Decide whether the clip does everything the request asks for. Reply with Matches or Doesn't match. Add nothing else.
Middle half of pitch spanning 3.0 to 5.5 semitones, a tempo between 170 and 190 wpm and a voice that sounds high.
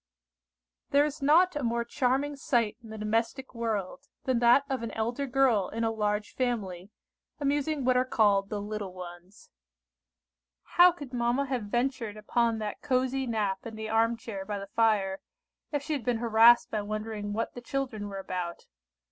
Matches